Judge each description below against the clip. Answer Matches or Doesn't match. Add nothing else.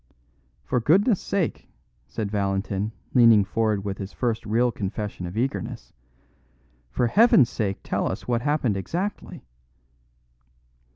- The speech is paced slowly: Matches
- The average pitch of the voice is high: Doesn't match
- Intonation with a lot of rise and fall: Doesn't match